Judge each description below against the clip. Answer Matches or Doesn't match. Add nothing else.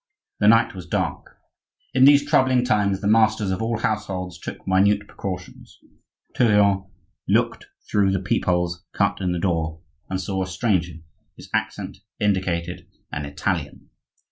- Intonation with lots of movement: Doesn't match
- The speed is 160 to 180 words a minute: Doesn't match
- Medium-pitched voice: Doesn't match